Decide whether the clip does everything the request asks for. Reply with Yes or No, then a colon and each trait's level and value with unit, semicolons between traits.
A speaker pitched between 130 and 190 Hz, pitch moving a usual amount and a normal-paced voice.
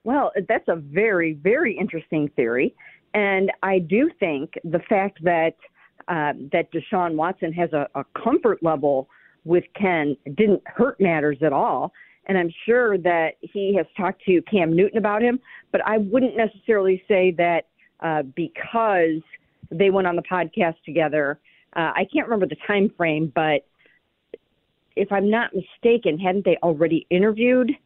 Yes: medium, 185 Hz; average, 4.6 semitones; average, 155 wpm